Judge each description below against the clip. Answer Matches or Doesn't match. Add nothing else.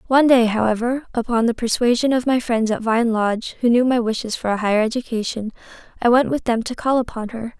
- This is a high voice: Matches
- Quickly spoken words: Matches